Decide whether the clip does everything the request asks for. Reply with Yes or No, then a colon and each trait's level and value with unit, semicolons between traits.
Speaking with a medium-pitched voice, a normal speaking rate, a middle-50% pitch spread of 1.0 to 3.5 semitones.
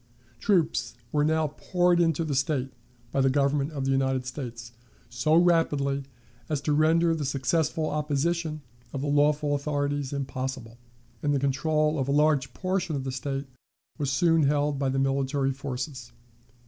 Yes: medium, 145 Hz; average, 160 wpm; narrow, 2.4 semitones